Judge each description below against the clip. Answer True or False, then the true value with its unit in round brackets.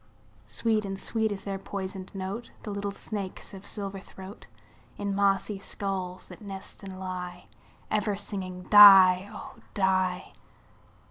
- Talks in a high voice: True (195 Hz)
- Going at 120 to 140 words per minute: True (135 wpm)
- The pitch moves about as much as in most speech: False (1.4 semitones)